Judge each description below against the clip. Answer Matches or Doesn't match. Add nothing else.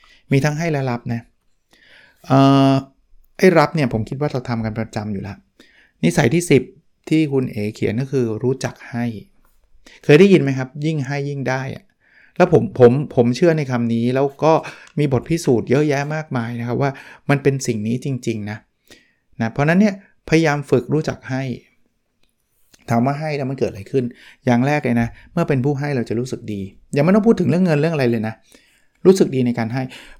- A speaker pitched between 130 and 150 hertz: Matches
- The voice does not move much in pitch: Doesn't match